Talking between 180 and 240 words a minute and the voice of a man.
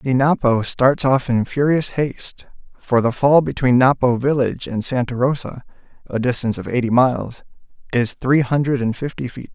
No: average, 170 wpm; male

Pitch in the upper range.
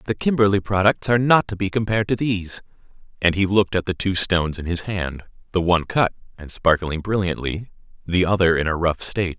No: very low, 95 Hz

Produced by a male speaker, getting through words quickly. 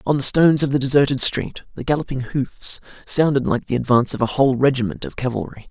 Yes: male; fast, 210 wpm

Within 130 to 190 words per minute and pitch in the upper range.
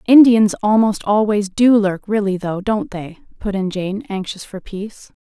Yes: average, 170 wpm; high, 205 Hz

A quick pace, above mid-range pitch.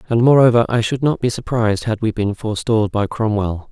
No: fast, 210 wpm; low, 115 Hz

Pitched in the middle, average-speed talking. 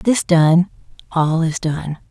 Yes: medium, 165 Hz; average, 145 wpm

